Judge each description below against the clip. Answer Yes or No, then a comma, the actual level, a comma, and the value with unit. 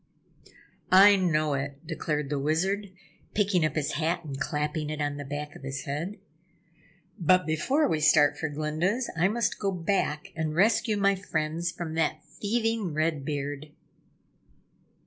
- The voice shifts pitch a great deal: No, average, 4.3 semitones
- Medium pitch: Yes, medium, 160 Hz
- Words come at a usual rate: Yes, average, 150 wpm